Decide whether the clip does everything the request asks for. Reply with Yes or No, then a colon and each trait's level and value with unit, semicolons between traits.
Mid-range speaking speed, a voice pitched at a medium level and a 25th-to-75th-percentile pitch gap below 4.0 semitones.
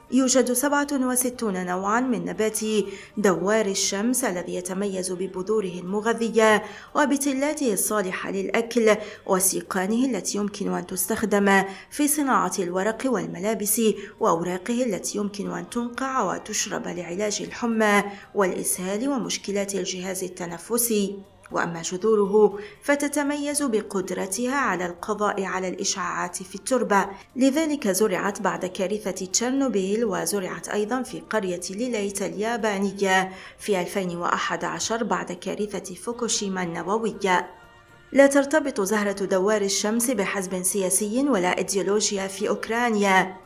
No: average, 100 wpm; high, 205 Hz; average, 3.5 semitones